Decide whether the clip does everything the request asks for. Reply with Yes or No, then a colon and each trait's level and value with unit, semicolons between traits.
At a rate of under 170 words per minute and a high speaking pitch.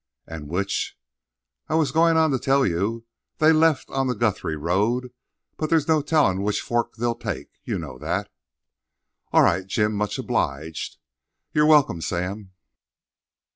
No: average, 145 wpm; low, 115 Hz